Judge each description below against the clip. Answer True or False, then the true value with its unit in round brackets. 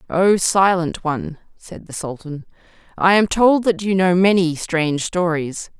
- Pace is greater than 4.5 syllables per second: False (4.3 syllables/s)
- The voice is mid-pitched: True (175 Hz)